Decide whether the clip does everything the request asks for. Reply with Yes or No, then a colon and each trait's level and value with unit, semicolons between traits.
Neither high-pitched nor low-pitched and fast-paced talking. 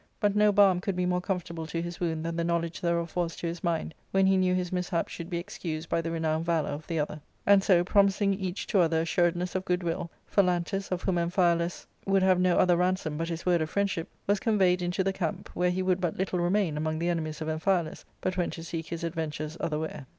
Yes: medium, 175 Hz; fast, 240 wpm